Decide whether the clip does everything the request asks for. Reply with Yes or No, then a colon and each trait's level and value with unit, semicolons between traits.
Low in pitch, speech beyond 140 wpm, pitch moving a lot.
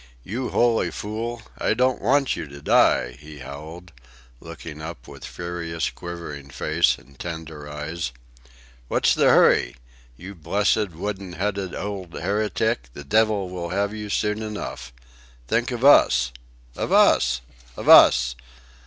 No: very low, 85 Hz; slow, 135 wpm; wide, 5.9 semitones